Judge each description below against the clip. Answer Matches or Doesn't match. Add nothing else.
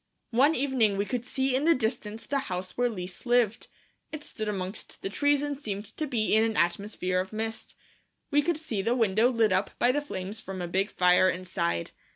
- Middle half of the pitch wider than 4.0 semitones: Matches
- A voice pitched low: Doesn't match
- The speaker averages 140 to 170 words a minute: Doesn't match